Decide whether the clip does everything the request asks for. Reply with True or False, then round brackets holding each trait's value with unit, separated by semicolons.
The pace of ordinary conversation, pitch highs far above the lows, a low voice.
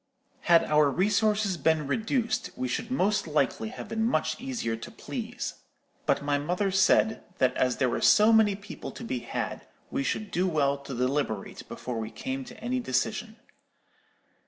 False (170 wpm; 8.1 semitones; 180 Hz)